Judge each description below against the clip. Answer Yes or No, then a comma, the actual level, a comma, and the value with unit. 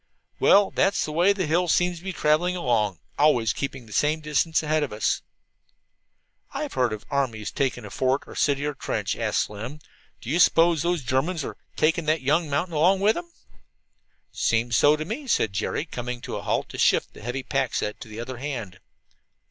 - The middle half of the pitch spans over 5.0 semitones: Yes, wide, 5.4 semitones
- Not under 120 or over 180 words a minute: No, fast, 205 wpm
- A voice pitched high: No, medium, 145 Hz